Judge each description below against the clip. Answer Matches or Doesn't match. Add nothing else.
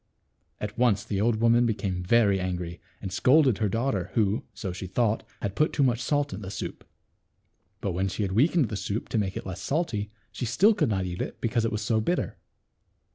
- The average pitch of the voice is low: Matches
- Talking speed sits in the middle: Doesn't match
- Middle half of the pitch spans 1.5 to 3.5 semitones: Doesn't match